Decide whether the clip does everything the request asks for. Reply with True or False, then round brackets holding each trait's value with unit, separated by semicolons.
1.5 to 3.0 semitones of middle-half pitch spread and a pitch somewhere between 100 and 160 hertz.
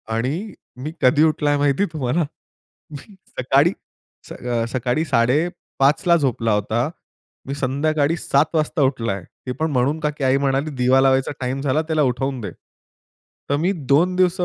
False (3.4 semitones; 140 Hz)